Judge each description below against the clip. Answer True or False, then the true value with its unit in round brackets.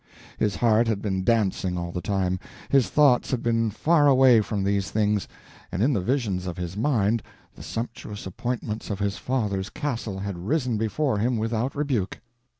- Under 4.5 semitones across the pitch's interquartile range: True (4.0 semitones)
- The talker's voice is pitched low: True (110 Hz)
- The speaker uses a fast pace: False (170 wpm)